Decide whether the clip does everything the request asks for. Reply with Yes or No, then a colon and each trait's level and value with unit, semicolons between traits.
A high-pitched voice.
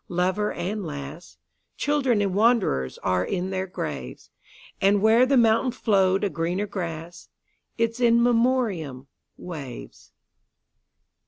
Yes: high, 195 Hz